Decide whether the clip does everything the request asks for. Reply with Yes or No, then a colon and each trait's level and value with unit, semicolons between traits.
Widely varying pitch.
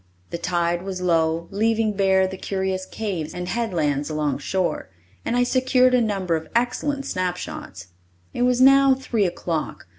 Yes: wide, 5.7 semitones